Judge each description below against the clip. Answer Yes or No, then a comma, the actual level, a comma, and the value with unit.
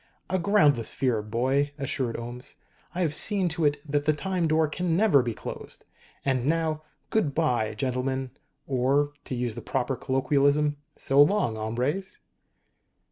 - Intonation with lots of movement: No, average, 4.0 semitones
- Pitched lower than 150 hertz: Yes, medium, 140 Hz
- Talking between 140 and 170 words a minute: Yes, average, 150 wpm